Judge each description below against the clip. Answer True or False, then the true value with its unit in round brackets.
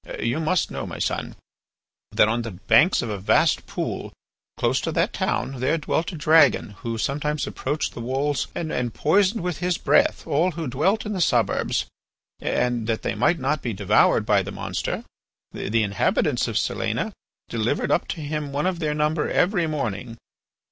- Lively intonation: True (5.9 semitones)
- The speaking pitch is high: False (150 Hz)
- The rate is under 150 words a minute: False (175 wpm)